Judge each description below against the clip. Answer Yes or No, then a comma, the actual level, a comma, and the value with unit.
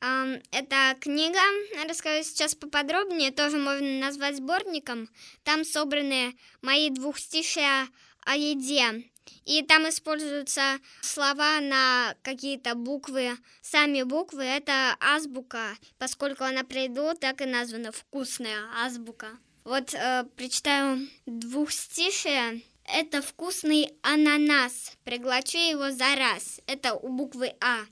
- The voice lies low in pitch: No, very high, 275 Hz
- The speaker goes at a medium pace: No, slow, 105 wpm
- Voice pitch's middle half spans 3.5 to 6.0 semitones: No, average, 2.7 semitones